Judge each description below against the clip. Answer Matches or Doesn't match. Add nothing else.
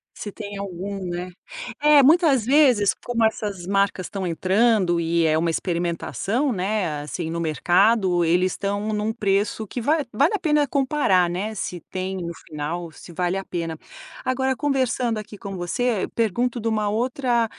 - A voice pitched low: Doesn't match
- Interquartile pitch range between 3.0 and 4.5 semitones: Doesn't match